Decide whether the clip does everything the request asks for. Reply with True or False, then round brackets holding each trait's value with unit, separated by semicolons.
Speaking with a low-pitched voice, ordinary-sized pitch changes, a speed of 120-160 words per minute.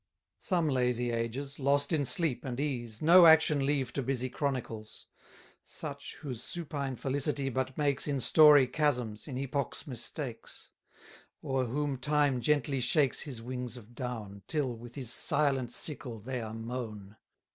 True (130 Hz; 3.1 semitones; 145 wpm)